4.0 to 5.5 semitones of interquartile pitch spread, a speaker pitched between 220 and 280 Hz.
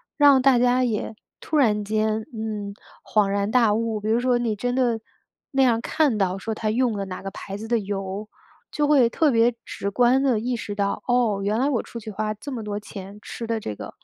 No: average, 3.1 semitones; high, 225 Hz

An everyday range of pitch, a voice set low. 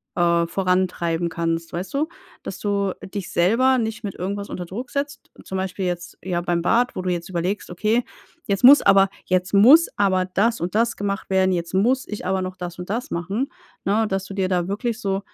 No: average, 3.2 semitones; high, 190 Hz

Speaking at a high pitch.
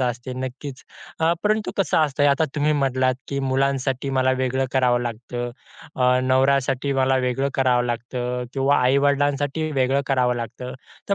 No: low, 130 Hz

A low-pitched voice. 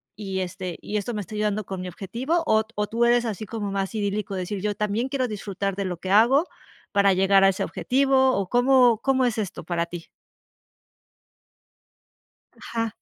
No: high, 210 Hz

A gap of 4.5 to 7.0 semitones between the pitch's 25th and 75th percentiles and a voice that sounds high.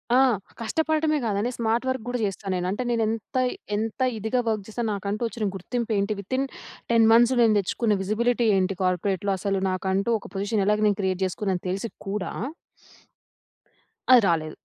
No: average, 3.3 semitones; high, 210 Hz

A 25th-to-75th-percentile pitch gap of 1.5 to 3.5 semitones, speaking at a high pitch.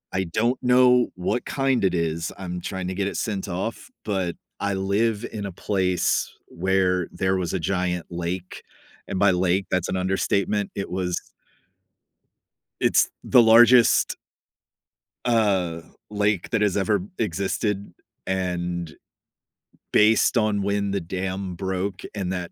No: narrow, 2.4 semitones; very low, 95 Hz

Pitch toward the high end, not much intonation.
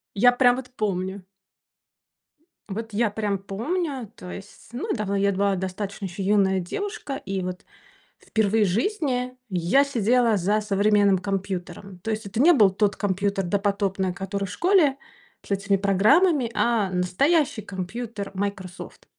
No: high, 200 Hz; average, 3.7 semitones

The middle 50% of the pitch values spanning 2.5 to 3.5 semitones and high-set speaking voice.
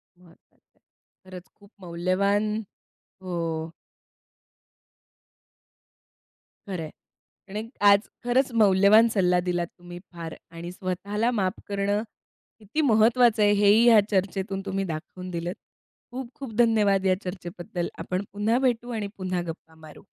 Yes: average, 3.2 semitones; high, 195 Hz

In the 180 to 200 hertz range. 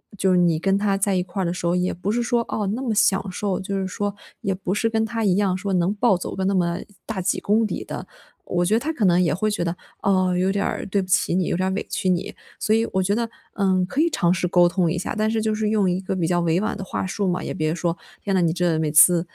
Yes: high, 190 Hz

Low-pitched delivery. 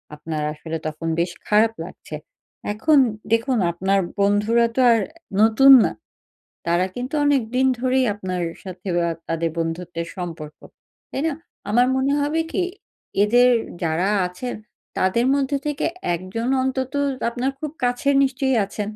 No: high, 220 Hz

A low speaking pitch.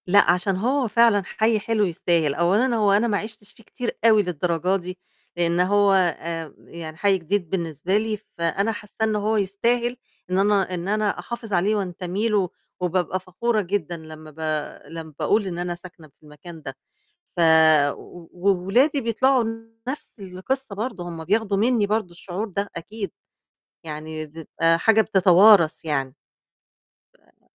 No: high, 195 Hz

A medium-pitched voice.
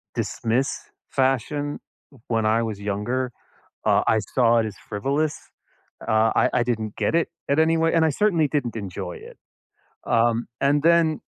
No: low, 125 Hz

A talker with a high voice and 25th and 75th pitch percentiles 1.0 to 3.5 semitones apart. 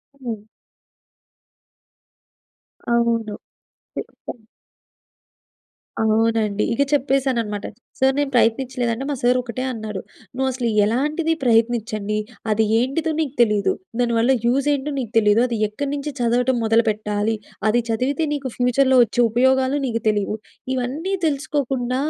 Yes: high, 240 Hz; average, 3.1 semitones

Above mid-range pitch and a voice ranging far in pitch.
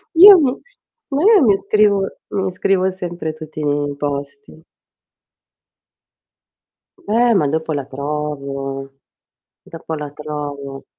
No: medium, 155 Hz; wide, 5.7 semitones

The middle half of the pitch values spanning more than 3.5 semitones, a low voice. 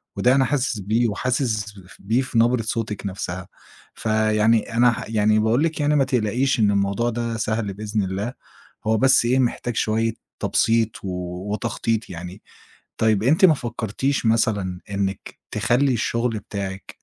No: average, 2.8 semitones; low, 110 Hz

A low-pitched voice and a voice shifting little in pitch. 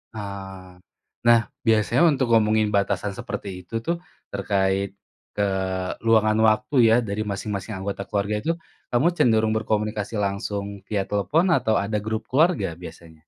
Yes: low, 105 Hz; narrow, 2.0 semitones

